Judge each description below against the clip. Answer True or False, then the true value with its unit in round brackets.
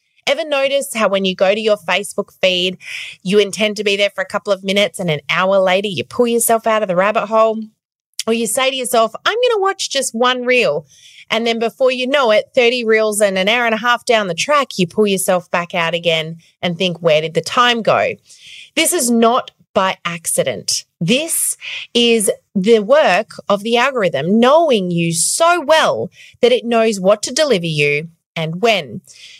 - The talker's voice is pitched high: True (215 Hz)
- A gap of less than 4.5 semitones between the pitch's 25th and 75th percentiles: False (5.3 semitones)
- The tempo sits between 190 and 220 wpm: True (200 wpm)